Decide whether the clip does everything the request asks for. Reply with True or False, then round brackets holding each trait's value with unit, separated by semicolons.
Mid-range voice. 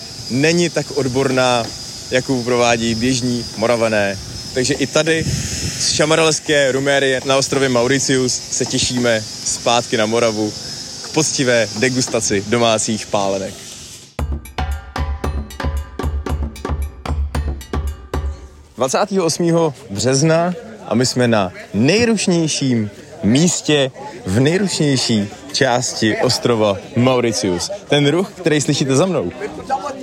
False (125 Hz)